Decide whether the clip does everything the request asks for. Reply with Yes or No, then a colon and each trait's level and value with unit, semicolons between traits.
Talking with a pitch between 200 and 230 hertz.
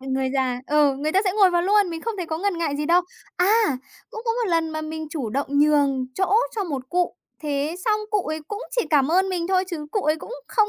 No: very high, 330 Hz